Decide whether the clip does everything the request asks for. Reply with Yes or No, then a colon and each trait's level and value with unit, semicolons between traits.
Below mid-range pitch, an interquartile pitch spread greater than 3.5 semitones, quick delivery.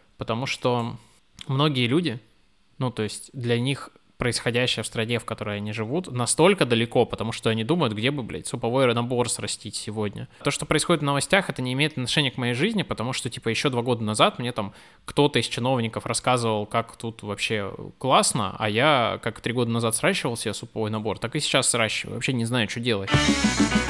No: low, 120 Hz; average, 3.1 semitones; fast, 195 wpm